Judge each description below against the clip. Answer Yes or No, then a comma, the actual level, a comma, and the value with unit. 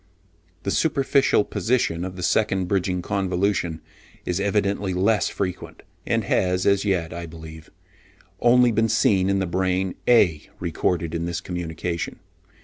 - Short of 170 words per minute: Yes, average, 140 wpm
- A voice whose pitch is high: No, very low, 95 Hz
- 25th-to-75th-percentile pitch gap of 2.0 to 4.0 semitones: Yes, average, 2.7 semitones